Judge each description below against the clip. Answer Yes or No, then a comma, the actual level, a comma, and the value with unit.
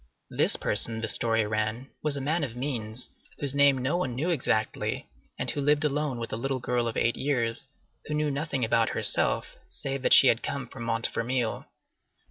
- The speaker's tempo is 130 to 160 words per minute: No, average, 190 wpm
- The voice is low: Yes, low, 130 Hz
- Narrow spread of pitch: No, average, 3.7 semitones